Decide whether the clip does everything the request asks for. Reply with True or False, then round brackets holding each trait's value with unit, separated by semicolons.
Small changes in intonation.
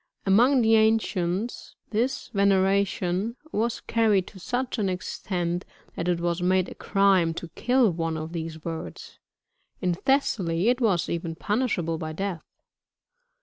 False (4.5 semitones)